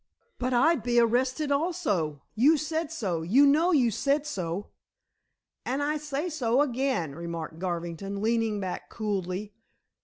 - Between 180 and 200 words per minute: No, average, 140 wpm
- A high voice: Yes, high, 240 Hz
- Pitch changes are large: Yes, wide, 7.4 semitones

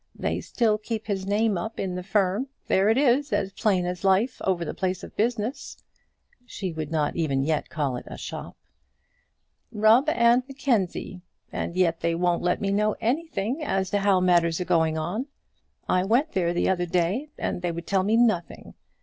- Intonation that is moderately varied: Yes, average, 4.3 semitones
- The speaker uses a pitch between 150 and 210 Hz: Yes, high, 190 Hz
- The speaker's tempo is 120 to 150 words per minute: No, average, 190 wpm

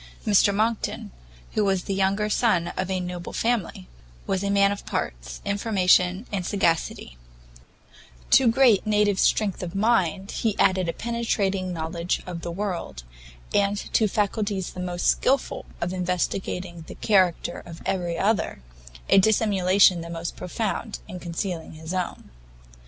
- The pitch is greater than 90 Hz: Yes, high, 190 Hz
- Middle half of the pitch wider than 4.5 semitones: No, average, 2.9 semitones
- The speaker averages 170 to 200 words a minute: No, average, 145 wpm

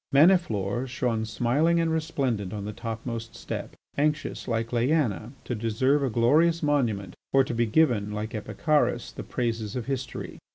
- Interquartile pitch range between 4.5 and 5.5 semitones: Yes, average, 4.8 semitones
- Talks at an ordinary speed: Yes, average, 155 wpm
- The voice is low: Yes, low, 120 Hz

